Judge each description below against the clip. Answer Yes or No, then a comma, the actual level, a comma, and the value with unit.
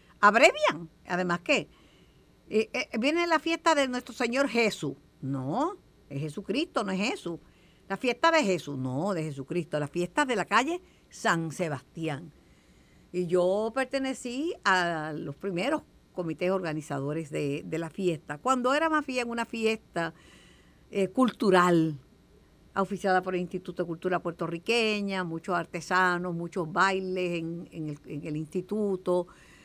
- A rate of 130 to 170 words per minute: Yes, average, 140 wpm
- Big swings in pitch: Yes, wide, 5.9 semitones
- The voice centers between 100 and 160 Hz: No, medium, 185 Hz